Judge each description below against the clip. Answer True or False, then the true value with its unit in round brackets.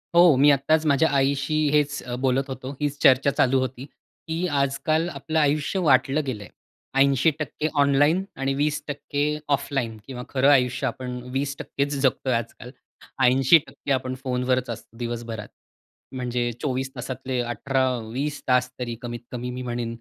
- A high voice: False (135 Hz)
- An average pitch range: False (2.3 semitones)